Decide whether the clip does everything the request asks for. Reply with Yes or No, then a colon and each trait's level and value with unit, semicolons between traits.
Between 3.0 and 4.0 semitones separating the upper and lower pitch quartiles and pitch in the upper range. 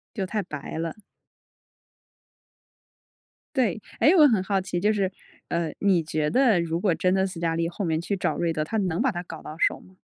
No: average, 3.5 semitones; medium, 180 Hz